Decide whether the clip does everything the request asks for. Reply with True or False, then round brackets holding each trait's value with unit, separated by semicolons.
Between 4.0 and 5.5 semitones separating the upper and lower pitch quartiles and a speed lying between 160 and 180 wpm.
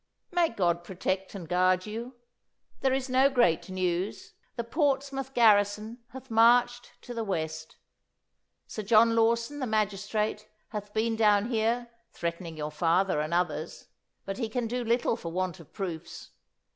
False (4.6 semitones; 150 wpm)